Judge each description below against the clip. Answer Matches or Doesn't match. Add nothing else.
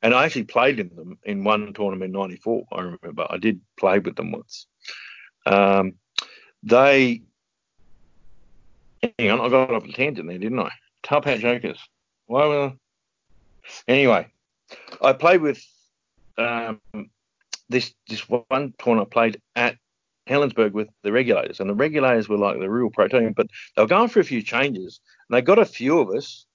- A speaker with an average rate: Matches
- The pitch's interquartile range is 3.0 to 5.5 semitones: Matches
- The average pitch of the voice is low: Matches